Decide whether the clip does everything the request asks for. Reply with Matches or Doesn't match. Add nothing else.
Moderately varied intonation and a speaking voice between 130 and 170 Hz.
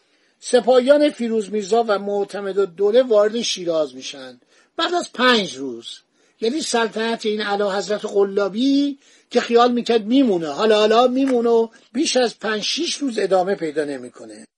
Doesn't match